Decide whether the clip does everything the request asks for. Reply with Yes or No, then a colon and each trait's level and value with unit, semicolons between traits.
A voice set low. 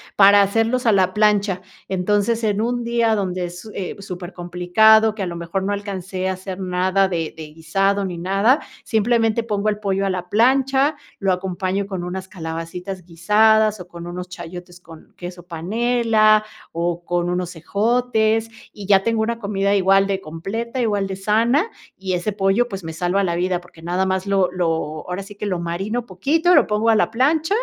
No: high, 195 Hz